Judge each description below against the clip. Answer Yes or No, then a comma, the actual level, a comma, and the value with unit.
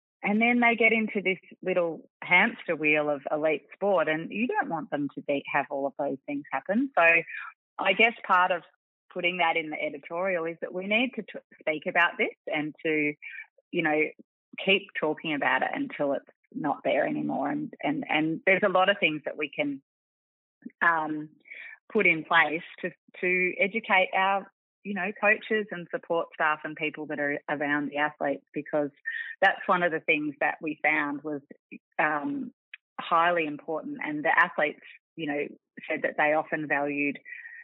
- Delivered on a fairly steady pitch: No, average, 4.9 semitones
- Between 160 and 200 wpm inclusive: Yes, average, 180 wpm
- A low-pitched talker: No, medium, 170 Hz